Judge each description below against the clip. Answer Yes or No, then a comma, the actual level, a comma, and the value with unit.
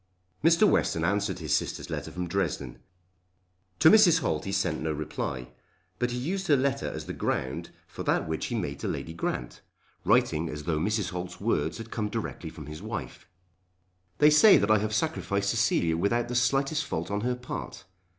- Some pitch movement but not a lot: No, wide, 7.0 semitones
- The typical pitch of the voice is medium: No, low, 100 Hz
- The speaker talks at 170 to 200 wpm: Yes, average, 190 wpm